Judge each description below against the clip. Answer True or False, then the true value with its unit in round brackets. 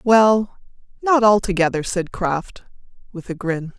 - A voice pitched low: False (195 Hz)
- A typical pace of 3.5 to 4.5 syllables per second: True (4.0 syllables/s)